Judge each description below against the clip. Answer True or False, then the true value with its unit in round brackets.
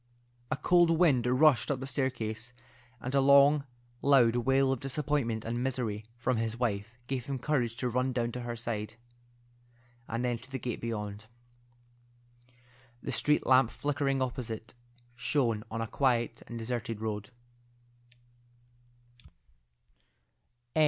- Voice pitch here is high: False (125 Hz)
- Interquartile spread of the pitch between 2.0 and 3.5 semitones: True (2.9 semitones)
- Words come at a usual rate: False (130 wpm)